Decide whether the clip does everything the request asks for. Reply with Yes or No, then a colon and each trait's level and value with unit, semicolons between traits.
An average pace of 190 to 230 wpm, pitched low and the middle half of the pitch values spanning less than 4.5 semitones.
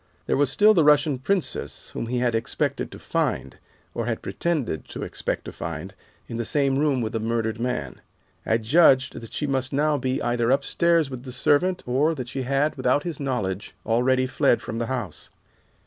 Yes: average, 195 wpm; low, 130 Hz; average, 3.8 semitones